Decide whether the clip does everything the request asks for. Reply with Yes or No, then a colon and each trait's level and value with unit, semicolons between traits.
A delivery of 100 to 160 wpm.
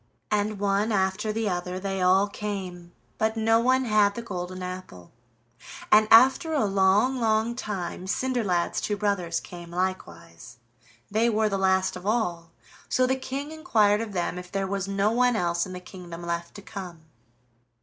No: average, 170 wpm